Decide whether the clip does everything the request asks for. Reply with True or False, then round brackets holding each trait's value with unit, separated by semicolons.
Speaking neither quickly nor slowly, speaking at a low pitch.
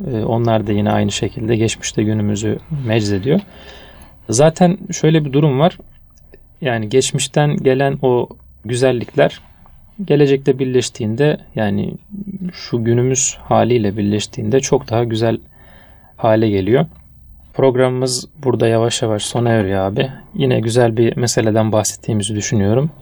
True (110 wpm; 115 Hz)